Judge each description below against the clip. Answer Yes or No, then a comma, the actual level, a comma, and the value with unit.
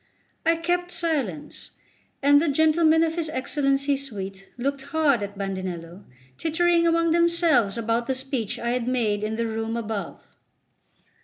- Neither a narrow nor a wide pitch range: No, wide, 6.5 semitones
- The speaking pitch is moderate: No, very high, 270 Hz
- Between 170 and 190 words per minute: No, average, 145 wpm